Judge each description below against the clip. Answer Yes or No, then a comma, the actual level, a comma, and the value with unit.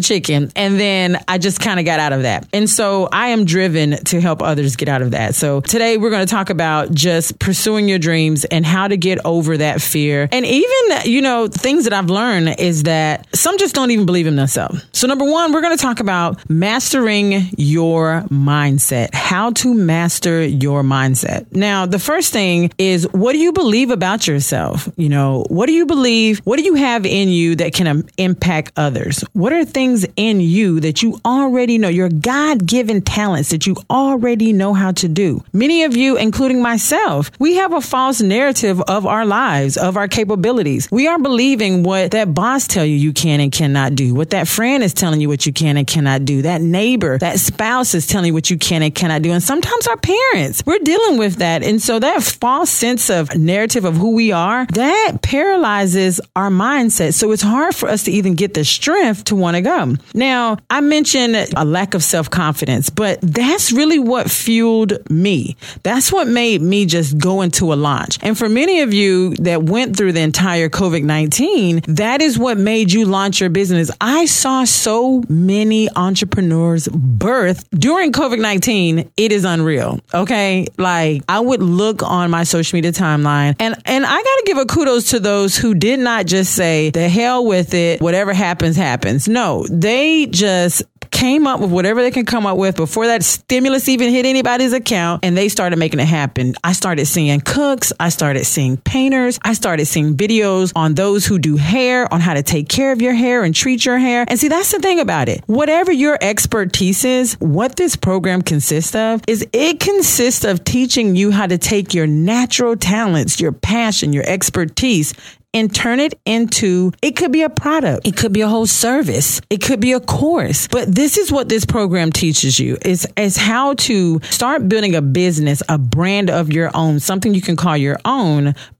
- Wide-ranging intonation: Yes, wide, 6.6 semitones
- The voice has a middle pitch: No, high, 195 Hz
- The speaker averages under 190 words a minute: No, average, 200 wpm